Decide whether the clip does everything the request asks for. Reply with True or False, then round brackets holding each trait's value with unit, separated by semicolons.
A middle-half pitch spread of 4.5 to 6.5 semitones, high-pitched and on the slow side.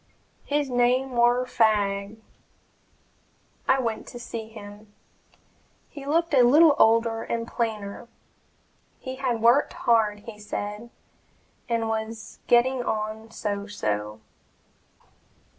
False (2.7 semitones; 230 Hz; 110 wpm)